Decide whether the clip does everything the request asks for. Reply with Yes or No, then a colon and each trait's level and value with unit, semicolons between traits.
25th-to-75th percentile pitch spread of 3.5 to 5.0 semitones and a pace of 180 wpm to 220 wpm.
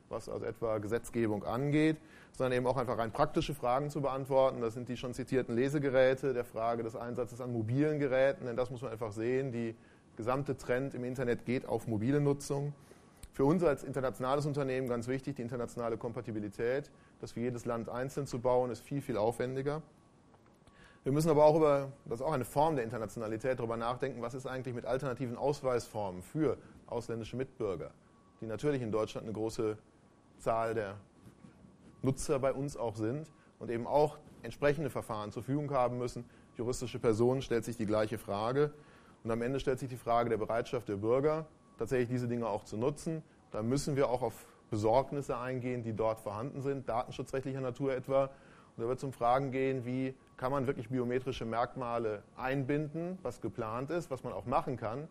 No: average, 2.8 semitones; average, 185 wpm